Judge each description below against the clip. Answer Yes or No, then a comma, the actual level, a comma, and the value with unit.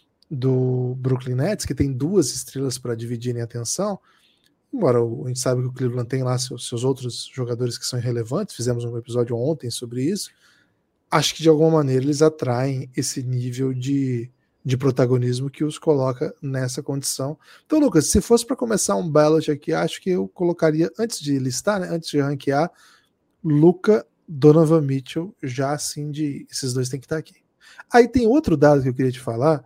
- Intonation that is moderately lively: Yes, average, 3.9 semitones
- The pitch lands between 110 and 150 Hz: Yes, medium, 140 Hz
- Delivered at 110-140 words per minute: No, fast, 185 wpm